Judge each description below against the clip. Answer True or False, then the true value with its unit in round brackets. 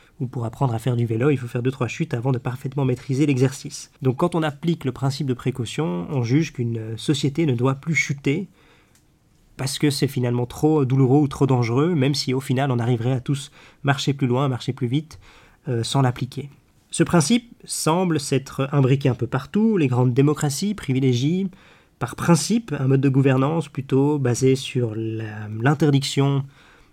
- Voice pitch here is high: False (135 Hz)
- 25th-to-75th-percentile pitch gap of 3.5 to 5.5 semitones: False (2.8 semitones)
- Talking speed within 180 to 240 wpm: True (185 wpm)